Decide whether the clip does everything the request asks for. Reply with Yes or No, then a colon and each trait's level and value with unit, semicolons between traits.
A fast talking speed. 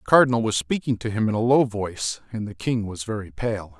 Yes: fast, 255 wpm